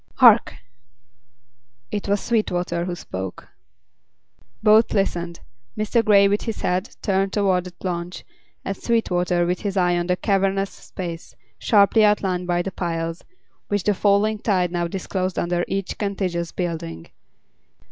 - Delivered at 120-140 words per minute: Yes, slow, 135 wpm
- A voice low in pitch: No, medium, 185 Hz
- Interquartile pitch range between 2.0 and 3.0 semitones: Yes, narrow, 2.5 semitones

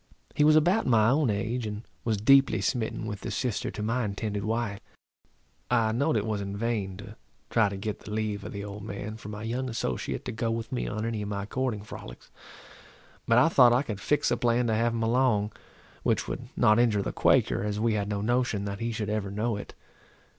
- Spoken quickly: Yes, fast, 225 wpm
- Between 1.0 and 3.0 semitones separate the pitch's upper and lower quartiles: Yes, narrow, 2.6 semitones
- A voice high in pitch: No, low, 110 Hz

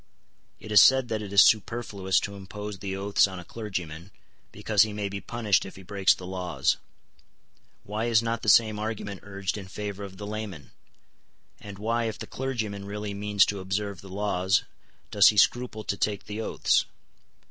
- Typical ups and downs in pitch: No, narrow, 1.9 semitones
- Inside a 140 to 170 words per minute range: No, average, 185 wpm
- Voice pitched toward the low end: Yes, low, 100 Hz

